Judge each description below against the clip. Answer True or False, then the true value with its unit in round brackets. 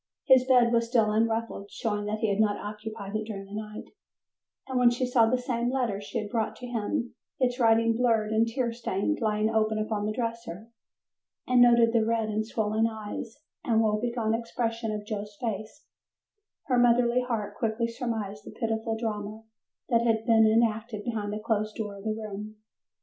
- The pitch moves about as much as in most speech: False (1.8 semitones)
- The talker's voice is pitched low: False (225 Hz)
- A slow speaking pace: False (185 wpm)